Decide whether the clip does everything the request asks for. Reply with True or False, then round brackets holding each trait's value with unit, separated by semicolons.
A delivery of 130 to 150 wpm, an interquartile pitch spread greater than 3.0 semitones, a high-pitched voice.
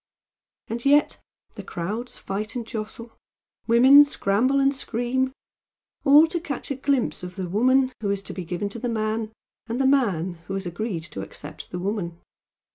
False (175 wpm; 5.2 semitones; 225 Hz)